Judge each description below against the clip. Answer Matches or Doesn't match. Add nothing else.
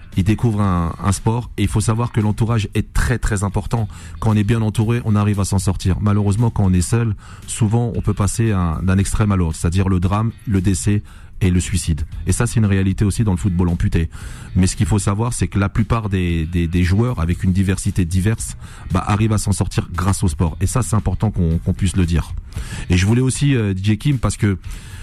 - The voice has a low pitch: Matches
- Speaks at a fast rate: Matches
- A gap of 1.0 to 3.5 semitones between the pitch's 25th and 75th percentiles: Matches